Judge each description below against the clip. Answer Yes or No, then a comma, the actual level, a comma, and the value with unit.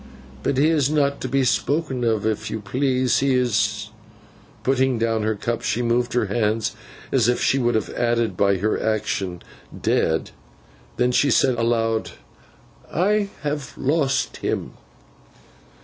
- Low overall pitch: Yes, low, 120 Hz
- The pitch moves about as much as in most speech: Yes, average, 3.6 semitones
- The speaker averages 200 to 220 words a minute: No, average, 150 wpm